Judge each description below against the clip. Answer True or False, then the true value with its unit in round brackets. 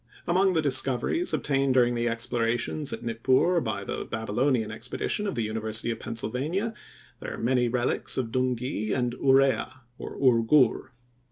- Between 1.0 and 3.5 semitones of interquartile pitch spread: True (2.9 semitones)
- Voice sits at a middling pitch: False (125 Hz)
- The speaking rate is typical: True (155 wpm)